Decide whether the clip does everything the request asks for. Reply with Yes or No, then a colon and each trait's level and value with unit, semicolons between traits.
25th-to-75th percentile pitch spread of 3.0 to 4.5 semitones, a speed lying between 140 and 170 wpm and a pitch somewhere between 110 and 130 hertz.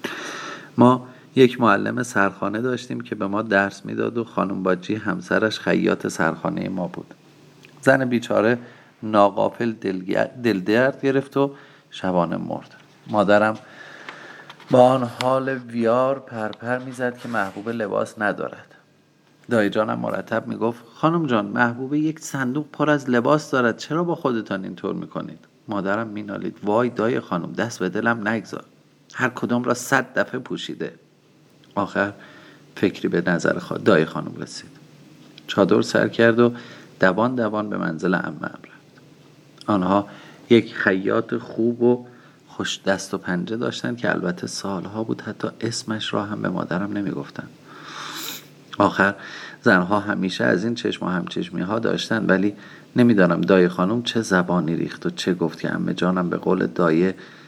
Yes: average, 4.1 semitones; average, 145 wpm; low, 115 Hz